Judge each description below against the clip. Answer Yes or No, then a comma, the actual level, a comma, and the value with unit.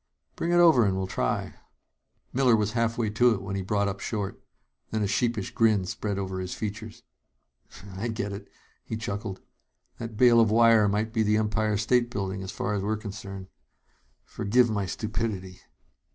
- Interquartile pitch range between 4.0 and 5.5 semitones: No, narrow, 2.6 semitones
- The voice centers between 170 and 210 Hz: No, low, 105 Hz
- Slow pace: No, average, 180 wpm